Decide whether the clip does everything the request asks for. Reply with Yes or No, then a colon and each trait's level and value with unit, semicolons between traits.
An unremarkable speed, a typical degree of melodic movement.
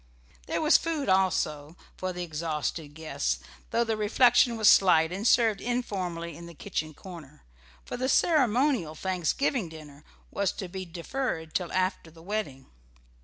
No: average, 150 wpm; wide, 5.8 semitones